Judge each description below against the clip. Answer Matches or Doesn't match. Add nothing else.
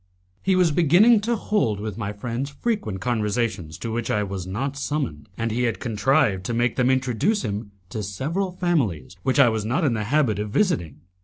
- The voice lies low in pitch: Matches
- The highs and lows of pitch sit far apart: Matches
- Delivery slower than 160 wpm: Doesn't match